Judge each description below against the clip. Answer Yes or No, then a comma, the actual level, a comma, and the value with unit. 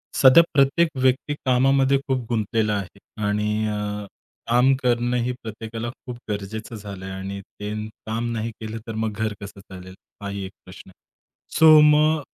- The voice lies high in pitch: No, low, 110 Hz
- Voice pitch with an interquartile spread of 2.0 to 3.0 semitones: No, average, 3.6 semitones